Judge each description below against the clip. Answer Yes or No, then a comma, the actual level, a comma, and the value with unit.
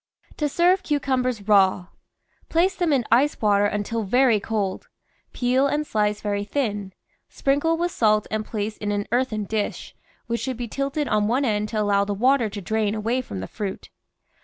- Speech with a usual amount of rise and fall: Yes, average, 4.6 semitones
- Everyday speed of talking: Yes, average, 180 wpm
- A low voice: No, high, 220 Hz